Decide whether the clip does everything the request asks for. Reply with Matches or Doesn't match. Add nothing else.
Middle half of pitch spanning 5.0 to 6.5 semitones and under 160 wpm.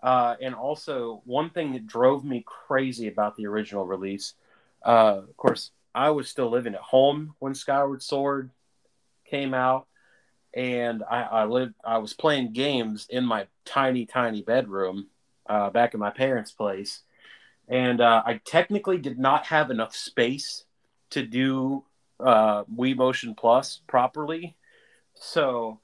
Doesn't match